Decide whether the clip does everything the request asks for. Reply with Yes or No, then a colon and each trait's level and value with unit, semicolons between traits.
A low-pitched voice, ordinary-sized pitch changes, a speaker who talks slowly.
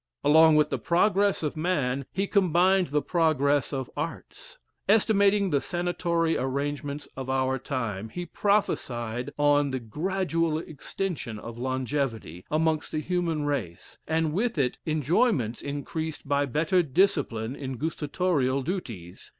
No: medium, 150 Hz; average, 4.8 semitones; slow, 130 wpm